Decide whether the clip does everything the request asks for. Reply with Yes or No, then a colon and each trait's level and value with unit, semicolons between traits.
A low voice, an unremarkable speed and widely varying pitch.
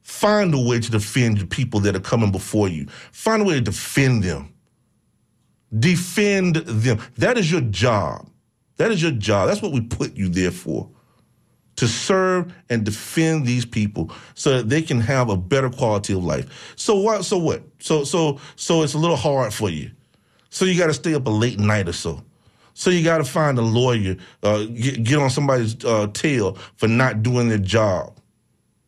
Yes: low, 120 Hz; average, 195 wpm; wide, 6.8 semitones